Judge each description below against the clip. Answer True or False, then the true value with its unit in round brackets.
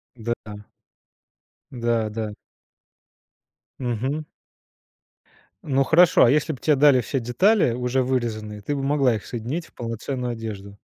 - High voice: False (125 Hz)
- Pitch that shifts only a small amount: False (3.5 semitones)